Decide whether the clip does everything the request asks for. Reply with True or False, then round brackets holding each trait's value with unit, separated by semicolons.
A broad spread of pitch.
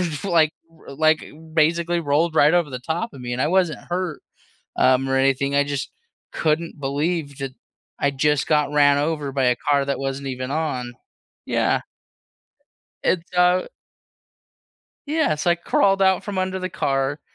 False (3.8 semitones)